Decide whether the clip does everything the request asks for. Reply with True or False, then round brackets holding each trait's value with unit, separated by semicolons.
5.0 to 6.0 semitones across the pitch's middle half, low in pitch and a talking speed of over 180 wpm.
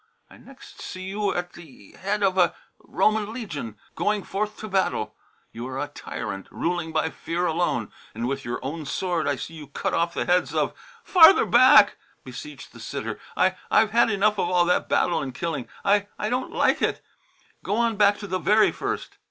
False (5.3 semitones; 180 Hz; 200 wpm)